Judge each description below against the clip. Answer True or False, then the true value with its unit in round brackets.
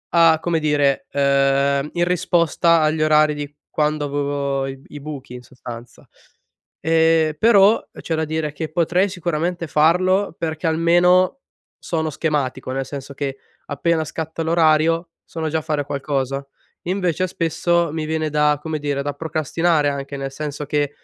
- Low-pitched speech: False (155 Hz)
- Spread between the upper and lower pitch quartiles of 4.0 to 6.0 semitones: False (2.7 semitones)